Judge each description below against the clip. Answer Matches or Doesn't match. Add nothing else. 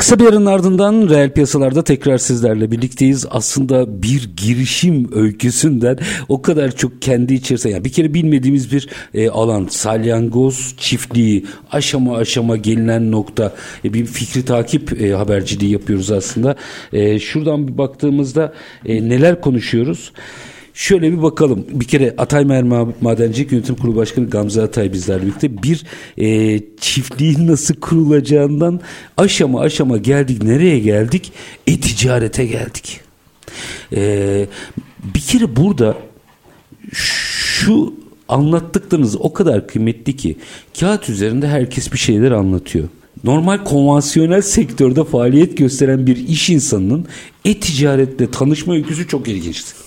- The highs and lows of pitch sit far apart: Doesn't match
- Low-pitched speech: Matches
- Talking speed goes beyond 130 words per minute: Doesn't match